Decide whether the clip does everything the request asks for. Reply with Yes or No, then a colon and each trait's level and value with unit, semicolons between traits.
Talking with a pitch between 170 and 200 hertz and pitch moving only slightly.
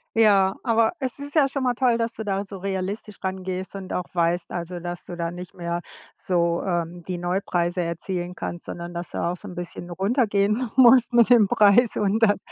No: high, 190 Hz; average, 4.3 semitones